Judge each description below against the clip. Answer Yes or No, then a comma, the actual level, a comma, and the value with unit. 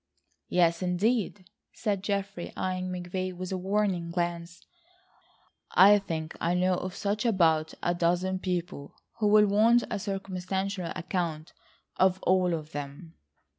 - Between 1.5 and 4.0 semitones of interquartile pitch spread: Yes, narrow, 2.4 semitones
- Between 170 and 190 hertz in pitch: Yes, medium, 185 Hz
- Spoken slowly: Yes, slow, 130 wpm